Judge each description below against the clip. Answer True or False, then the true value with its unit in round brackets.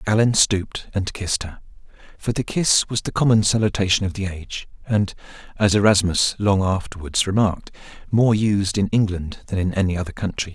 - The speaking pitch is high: False (100 Hz)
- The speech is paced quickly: False (170 wpm)